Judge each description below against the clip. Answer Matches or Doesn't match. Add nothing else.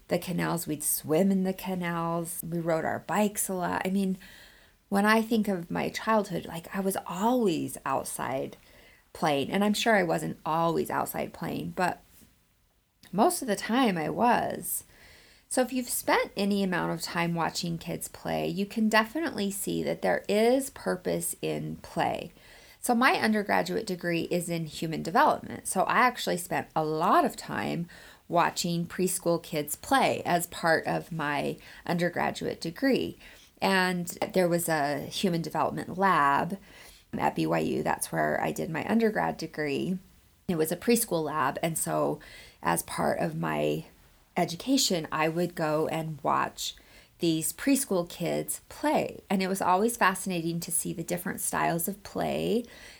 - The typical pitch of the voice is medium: Matches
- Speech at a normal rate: Matches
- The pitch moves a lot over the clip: Doesn't match